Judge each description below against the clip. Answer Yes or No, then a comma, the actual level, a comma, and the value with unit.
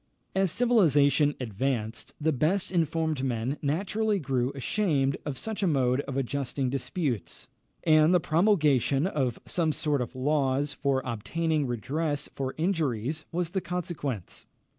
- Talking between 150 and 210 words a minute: No, slow, 135 wpm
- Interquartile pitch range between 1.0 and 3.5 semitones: No, average, 4.0 semitones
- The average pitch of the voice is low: No, medium, 145 Hz